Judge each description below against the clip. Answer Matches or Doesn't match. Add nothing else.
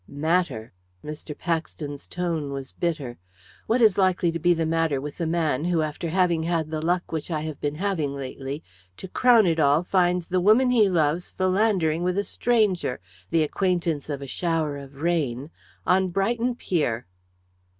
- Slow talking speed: Doesn't match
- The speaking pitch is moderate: Matches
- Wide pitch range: Doesn't match